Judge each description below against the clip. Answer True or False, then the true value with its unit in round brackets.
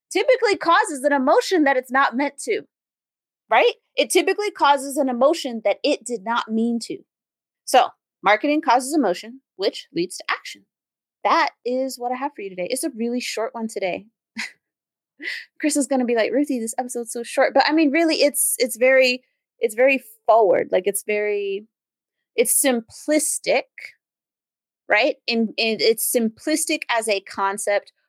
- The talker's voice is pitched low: False (265 Hz)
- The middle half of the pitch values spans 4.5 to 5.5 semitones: True (5.1 semitones)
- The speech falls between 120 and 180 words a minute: True (160 wpm)